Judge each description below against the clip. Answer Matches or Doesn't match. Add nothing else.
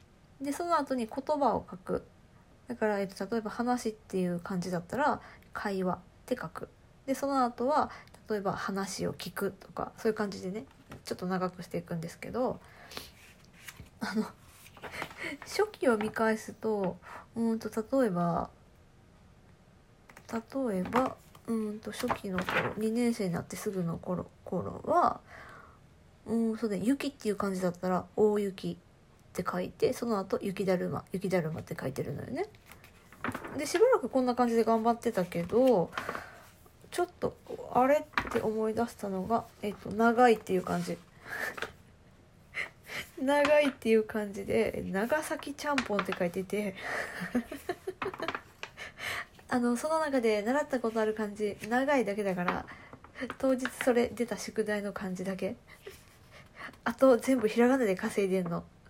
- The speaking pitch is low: Doesn't match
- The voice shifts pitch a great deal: Doesn't match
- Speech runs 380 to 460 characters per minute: Doesn't match